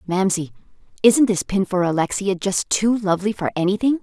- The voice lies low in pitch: No, high, 195 Hz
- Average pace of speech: Yes, average, 165 wpm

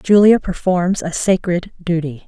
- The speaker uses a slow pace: Yes, slow, 130 wpm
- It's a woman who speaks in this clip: Yes, female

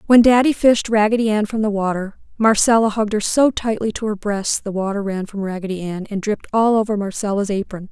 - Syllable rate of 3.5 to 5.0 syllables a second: No, 5.9 syllables/s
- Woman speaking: Yes, female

